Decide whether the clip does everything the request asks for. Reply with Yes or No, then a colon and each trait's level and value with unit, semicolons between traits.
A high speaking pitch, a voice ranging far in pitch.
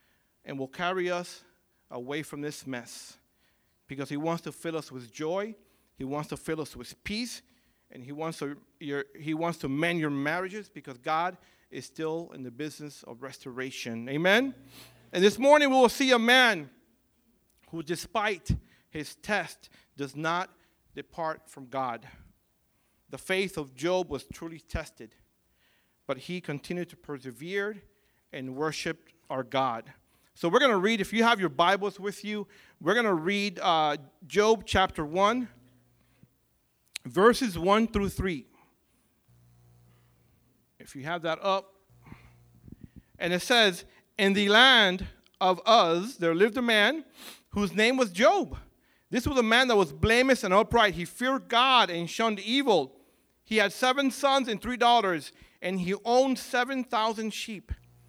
No: medium, 175 Hz; wide, 7.1 semitones